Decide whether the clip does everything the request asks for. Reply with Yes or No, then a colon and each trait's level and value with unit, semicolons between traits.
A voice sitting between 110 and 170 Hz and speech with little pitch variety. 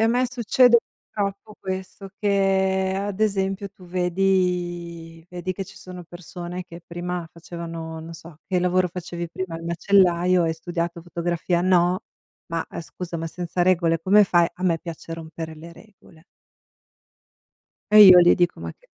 No: medium, 180 Hz; narrow, 2.1 semitones